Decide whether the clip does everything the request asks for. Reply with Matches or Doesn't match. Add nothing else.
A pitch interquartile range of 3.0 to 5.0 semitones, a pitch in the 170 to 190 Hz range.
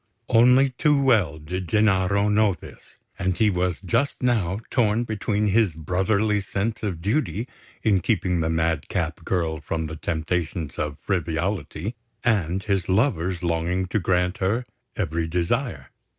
Doesn't match